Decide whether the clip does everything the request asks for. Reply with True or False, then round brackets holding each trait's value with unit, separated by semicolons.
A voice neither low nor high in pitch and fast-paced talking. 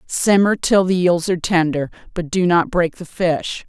False (175 Hz; 195 wpm)